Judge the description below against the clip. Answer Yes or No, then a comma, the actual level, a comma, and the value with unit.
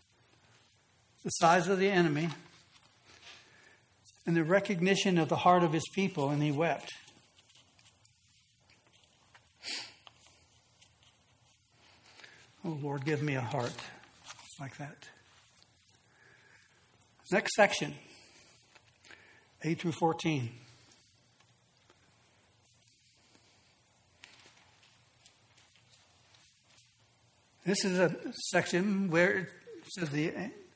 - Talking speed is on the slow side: Yes, slow, 75 wpm